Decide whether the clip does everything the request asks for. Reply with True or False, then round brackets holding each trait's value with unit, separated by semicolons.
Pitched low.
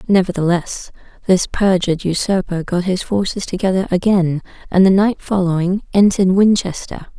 False (185 Hz)